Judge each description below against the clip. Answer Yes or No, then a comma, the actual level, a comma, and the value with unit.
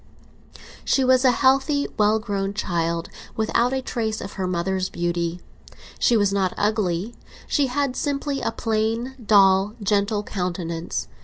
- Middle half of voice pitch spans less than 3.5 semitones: No, average, 4.8 semitones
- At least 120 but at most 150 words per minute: Yes, average, 140 wpm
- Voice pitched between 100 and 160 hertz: No, high, 210 Hz